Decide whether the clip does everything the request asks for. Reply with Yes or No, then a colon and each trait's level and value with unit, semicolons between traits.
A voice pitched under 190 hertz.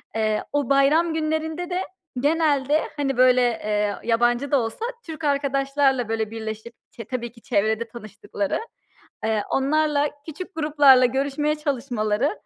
No: very high, 270 Hz